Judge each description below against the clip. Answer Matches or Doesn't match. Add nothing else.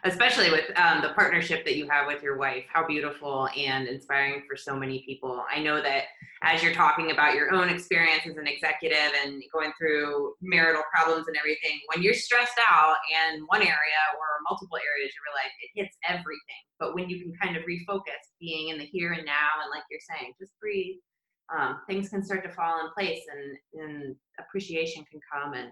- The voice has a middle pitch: Matches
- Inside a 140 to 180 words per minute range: Doesn't match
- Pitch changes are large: Doesn't match